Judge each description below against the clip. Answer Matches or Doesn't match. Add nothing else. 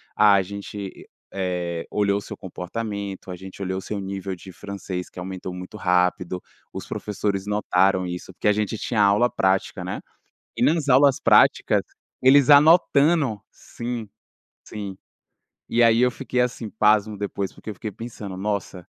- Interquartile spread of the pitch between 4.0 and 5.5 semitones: Doesn't match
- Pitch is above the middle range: Doesn't match